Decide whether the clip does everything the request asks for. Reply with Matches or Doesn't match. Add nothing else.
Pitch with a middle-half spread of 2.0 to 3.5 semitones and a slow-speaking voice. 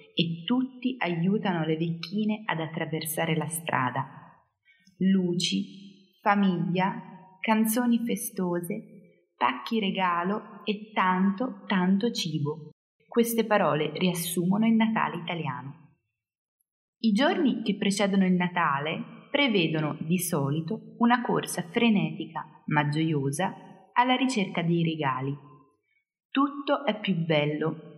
Doesn't match